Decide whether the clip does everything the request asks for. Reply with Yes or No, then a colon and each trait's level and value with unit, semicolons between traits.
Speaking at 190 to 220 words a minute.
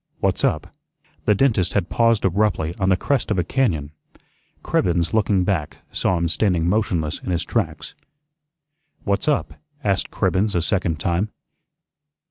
No: average, 145 wpm